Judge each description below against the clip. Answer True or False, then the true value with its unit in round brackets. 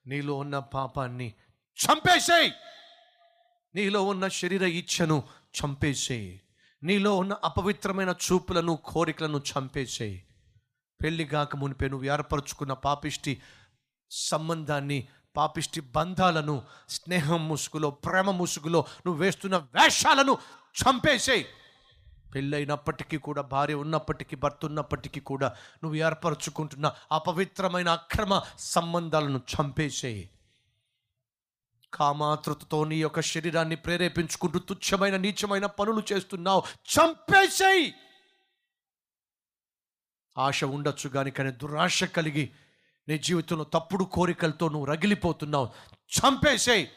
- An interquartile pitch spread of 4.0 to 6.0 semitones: True (4.3 semitones)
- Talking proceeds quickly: False (85 wpm)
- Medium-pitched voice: True (155 Hz)